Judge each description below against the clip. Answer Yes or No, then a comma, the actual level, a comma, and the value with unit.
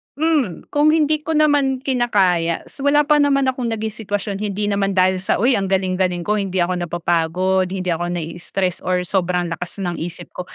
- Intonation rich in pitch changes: Yes, wide, 6.5 semitones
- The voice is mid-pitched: No, high, 195 Hz